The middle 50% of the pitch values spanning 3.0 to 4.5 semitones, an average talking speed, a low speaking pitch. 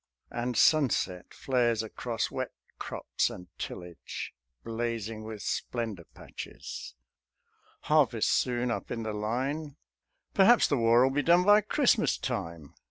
No: average, 4.1 semitones; slow, 125 wpm; low, 120 Hz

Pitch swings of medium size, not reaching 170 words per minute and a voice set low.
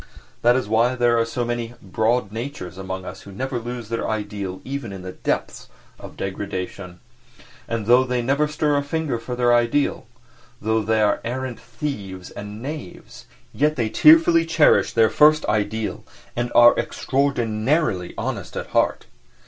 Yes: average, 4.1 semitones; average, 160 wpm; low, 120 Hz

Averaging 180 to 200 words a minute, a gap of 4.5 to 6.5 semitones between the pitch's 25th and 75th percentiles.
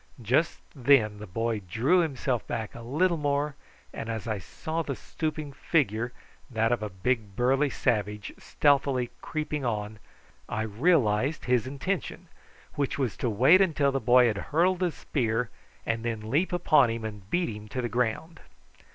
No: average, 165 wpm; average, 5.2 semitones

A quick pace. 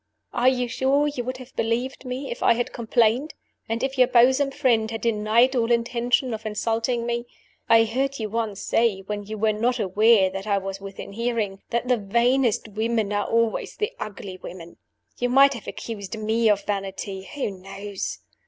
No: average, 185 wpm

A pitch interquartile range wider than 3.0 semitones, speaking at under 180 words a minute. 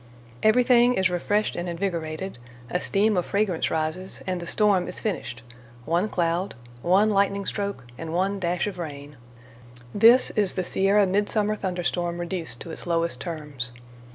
Yes: average, 3.4 semitones; average, 155 wpm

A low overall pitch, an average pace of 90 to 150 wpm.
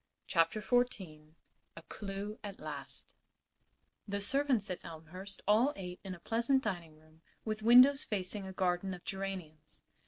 No: high, 195 Hz; average, 145 wpm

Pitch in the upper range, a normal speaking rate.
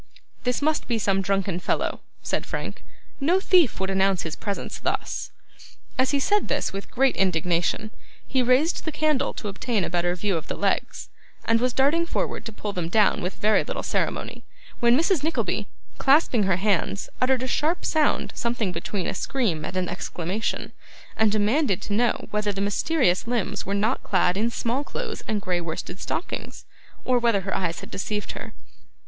Yes: high, 210 Hz; average, 180 wpm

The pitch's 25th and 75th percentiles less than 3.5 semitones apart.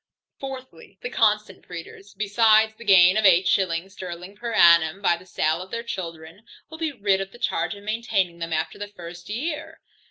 No: average, 4.0 semitones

